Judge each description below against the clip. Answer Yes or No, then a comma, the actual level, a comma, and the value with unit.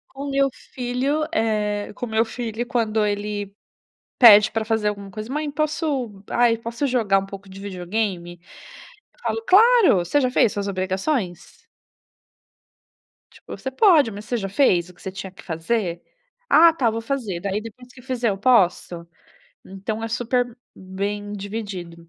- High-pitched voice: Yes, high, 215 Hz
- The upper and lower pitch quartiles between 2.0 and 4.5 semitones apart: Yes, average, 4.2 semitones